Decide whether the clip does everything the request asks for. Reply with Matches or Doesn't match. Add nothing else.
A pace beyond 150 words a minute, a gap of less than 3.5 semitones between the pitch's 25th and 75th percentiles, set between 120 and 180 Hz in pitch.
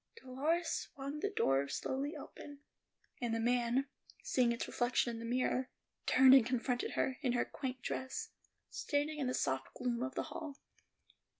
Doesn't match